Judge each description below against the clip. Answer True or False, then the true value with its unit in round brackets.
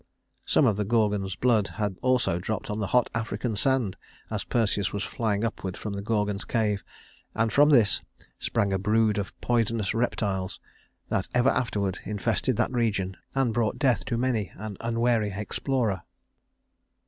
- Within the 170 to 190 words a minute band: False (160 wpm)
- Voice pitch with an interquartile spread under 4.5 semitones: True (2.8 semitones)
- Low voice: True (110 Hz)